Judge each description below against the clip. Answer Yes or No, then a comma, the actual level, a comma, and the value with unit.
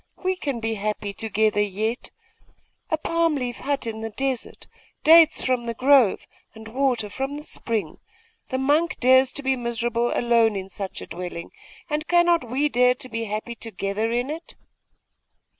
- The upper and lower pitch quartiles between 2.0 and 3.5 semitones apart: No, average, 4.1 semitones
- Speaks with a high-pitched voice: Yes, high, 240 Hz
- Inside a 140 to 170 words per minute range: Yes, average, 160 wpm